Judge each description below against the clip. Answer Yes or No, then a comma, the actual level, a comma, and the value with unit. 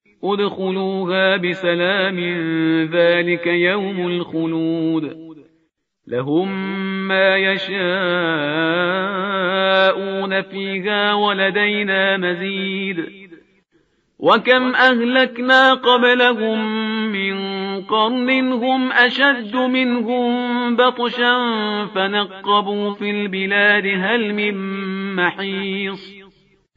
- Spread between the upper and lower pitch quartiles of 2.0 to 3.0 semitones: Yes, narrow, 2.6 semitones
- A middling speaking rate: No, slow, 60 wpm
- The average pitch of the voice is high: Yes, high, 195 Hz